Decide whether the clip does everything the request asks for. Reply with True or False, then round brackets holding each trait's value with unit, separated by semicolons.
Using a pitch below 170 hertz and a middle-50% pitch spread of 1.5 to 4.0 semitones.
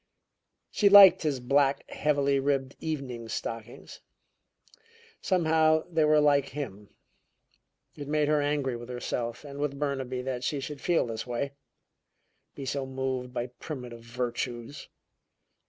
True (140 Hz; 3.1 semitones)